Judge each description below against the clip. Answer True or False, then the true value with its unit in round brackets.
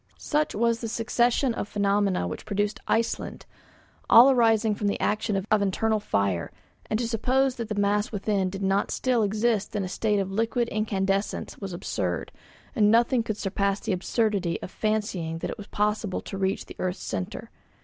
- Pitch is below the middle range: False (210 Hz)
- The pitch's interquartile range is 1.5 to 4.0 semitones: True (2.6 semitones)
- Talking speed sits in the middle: True (180 wpm)